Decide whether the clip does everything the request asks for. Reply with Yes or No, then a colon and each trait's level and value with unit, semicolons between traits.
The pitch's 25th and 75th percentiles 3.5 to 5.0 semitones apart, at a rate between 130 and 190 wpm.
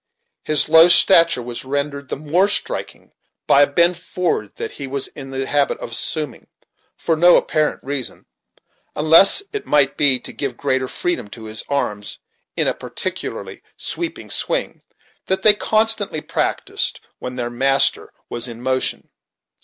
Yes: average, 4.4 semitones; average, 155 wpm